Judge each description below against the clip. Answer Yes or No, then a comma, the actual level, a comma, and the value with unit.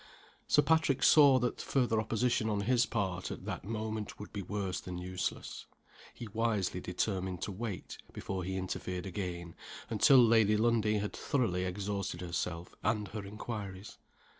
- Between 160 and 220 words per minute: No, average, 150 wpm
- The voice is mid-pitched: No, low, 105 Hz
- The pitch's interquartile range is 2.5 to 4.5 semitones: Yes, average, 3.6 semitones